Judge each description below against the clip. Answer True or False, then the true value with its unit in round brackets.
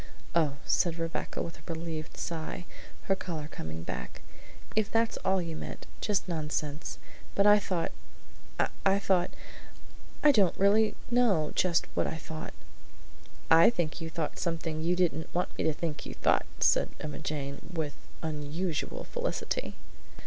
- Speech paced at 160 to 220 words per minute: False (150 wpm)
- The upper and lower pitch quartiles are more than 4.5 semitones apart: False (3.4 semitones)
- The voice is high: False (165 Hz)